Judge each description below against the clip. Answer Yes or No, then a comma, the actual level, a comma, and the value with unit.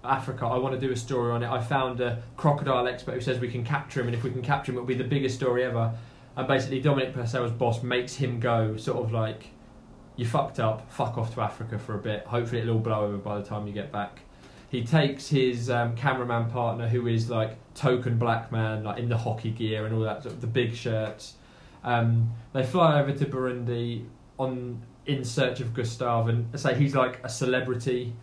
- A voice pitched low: Yes, low, 125 Hz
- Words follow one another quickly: Yes, fast, 225 wpm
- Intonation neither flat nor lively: No, narrow, 2.0 semitones